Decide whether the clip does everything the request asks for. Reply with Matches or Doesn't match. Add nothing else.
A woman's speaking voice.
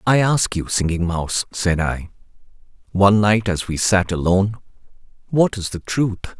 Doesn't match